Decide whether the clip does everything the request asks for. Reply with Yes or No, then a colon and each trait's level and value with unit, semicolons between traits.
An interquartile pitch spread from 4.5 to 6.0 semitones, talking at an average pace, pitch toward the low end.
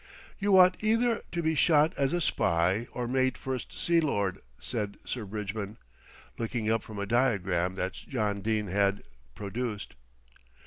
Yes: wide, 5.4 semitones; average, 150 wpm; low, 110 Hz